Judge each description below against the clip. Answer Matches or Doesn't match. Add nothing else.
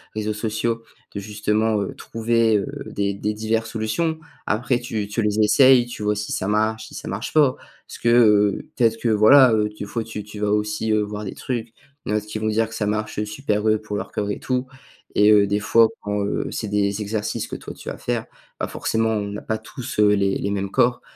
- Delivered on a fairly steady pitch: Matches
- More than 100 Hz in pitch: Matches